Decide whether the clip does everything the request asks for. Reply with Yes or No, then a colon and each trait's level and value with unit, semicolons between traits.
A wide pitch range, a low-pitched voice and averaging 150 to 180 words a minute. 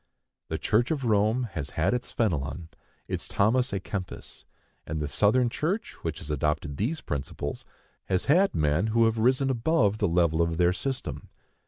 Yes: wide, 7.3 semitones; low, 100 Hz; average, 170 wpm